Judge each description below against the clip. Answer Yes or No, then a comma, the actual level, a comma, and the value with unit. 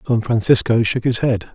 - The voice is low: Yes, low, 115 Hz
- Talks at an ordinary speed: Yes, average, 195 wpm